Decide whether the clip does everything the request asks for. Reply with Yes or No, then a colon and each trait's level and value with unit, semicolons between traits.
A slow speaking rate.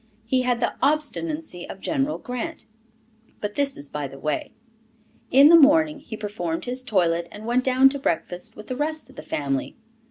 No: average, 185 wpm